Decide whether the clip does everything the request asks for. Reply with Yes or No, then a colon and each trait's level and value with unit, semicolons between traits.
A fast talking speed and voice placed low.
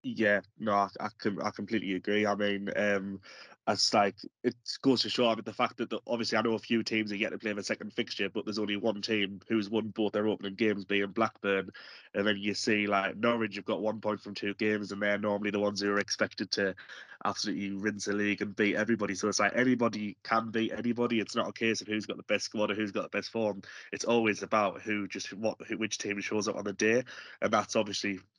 Yes: fast, 245 wpm; low, 105 Hz